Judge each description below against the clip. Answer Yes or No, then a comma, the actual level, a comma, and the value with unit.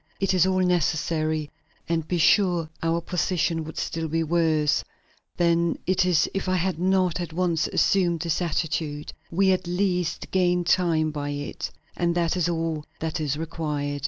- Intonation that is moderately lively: No, narrow, 2.3 semitones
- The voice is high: No, medium, 170 Hz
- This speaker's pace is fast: No, average, 165 wpm